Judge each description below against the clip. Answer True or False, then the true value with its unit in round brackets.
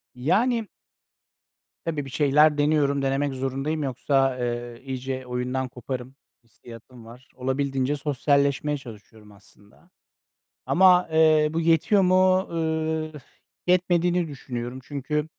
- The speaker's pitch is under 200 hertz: True (140 Hz)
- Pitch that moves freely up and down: False (3.7 semitones)